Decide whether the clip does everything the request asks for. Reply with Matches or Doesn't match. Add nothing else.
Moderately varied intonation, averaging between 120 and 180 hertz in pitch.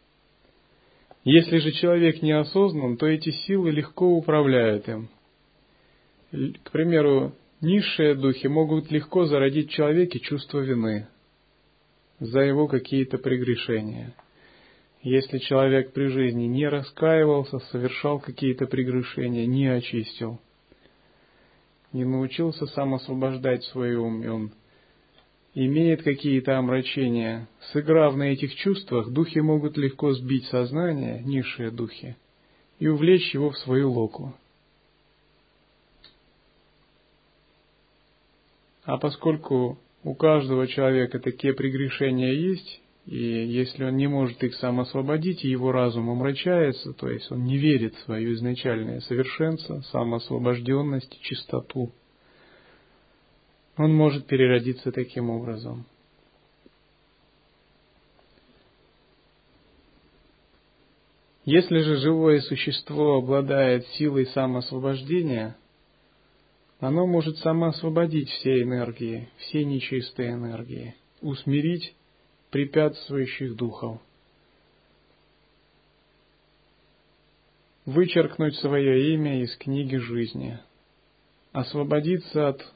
Matches